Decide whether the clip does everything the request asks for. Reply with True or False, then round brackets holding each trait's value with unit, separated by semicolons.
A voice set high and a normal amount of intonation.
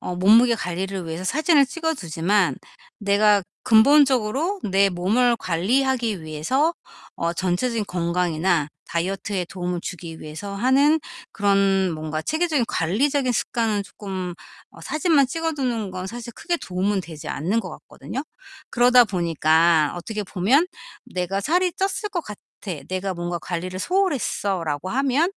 False (200 Hz; 6.5 semitones)